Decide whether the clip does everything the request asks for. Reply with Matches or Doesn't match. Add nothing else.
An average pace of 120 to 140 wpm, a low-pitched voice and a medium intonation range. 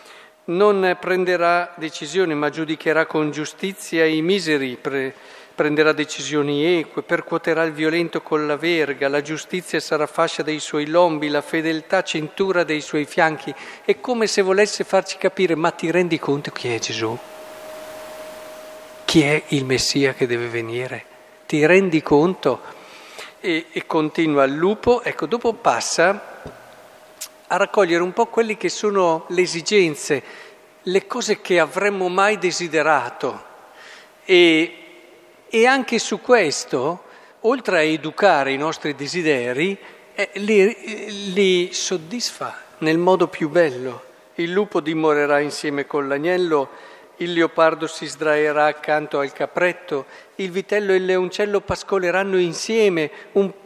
Doesn't match